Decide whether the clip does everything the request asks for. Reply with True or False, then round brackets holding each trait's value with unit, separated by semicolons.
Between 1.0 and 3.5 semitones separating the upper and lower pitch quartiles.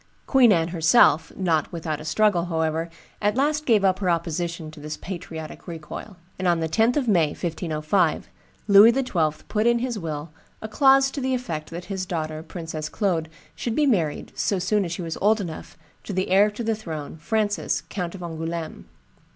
False (4.9 semitones)